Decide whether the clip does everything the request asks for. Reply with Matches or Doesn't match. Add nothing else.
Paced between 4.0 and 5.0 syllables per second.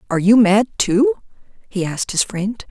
Doesn't match